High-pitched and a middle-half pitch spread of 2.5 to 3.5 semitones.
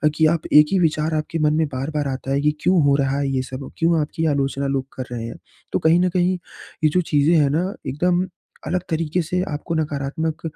No: medium, 150 Hz; average, 3.0 semitones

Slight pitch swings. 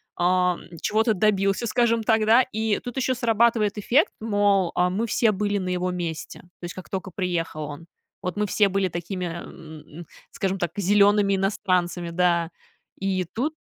No: average, 3.3 semitones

